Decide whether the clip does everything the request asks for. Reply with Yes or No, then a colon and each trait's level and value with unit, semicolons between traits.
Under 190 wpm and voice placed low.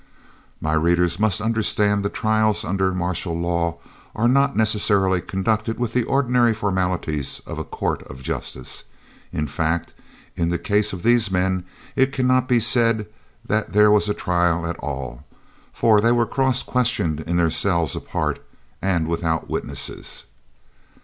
Yes: average, 150 wpm; low, 100 Hz